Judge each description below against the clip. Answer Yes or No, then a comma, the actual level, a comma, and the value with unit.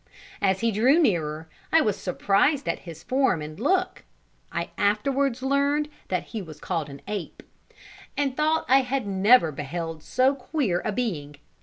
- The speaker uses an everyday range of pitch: No, wide, 8.2 semitones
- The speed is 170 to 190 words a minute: No, average, 160 wpm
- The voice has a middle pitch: No, high, 210 Hz